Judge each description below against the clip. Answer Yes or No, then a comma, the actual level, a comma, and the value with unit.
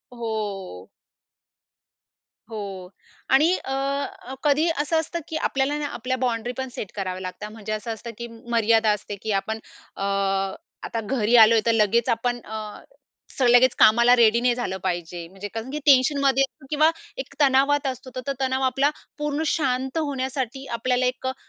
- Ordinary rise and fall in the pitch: Yes, average, 3.6 semitones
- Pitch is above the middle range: Yes, high, 245 Hz